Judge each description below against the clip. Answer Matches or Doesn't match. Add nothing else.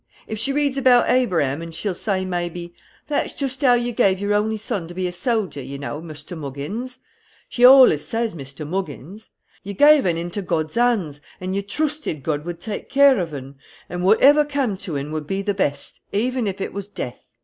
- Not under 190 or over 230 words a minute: Matches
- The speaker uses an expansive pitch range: Matches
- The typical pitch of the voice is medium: Doesn't match